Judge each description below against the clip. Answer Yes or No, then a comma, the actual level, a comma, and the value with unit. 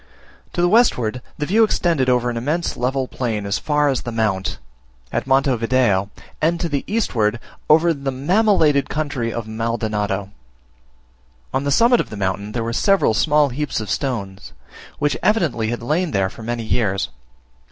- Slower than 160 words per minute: No, average, 170 wpm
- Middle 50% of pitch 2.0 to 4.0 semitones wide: No, wide, 5.5 semitones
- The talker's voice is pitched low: Yes, low, 130 Hz